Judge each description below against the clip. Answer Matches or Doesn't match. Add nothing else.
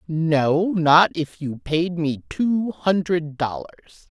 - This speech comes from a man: Doesn't match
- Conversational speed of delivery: Doesn't match